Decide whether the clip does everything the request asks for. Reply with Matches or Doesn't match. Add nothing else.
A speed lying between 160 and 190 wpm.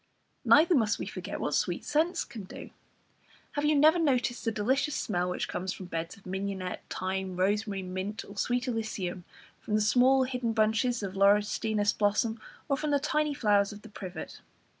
Matches